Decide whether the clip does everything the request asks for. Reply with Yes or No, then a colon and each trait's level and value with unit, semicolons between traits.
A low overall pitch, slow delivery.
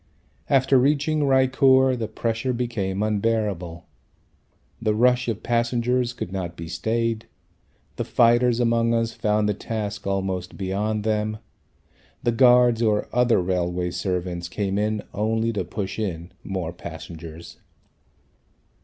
Yes: low, 110 Hz; slow, 125 wpm